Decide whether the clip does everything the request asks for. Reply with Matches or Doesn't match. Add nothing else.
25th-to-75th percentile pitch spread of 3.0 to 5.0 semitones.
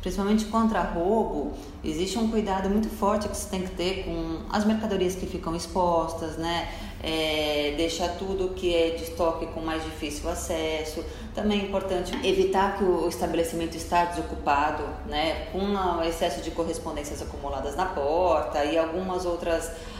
Doesn't match